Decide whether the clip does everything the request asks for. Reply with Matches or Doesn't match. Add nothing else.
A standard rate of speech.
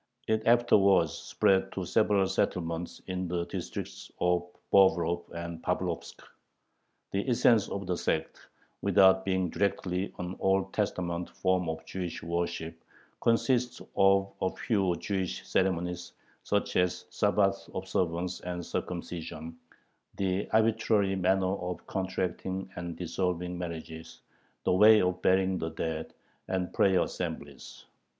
Doesn't match